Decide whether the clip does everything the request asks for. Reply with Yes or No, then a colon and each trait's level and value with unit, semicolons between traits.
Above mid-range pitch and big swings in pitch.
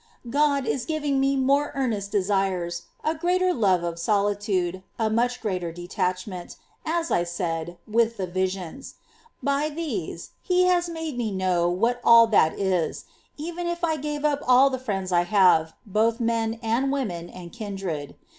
Yes: high, 220 Hz; wide, 7.1 semitones